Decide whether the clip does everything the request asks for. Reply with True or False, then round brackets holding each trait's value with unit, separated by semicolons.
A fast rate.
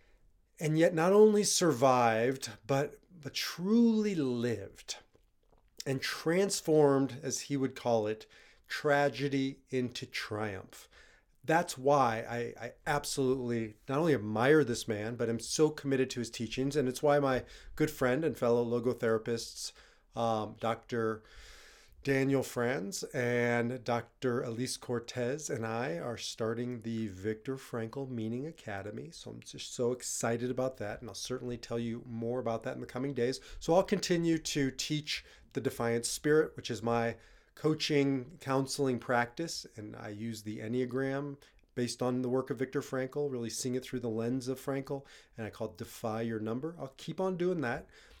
False (160 wpm)